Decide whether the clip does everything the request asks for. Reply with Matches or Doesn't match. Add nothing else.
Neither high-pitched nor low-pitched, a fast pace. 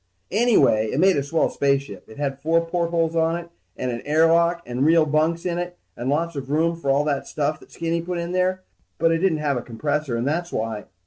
Matches